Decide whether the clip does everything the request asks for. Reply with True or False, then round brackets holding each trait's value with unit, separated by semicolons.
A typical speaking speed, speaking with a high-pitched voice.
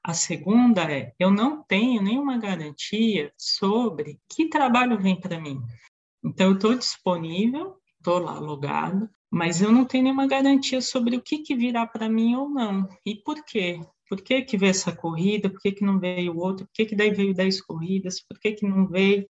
False (200 wpm; 200 Hz)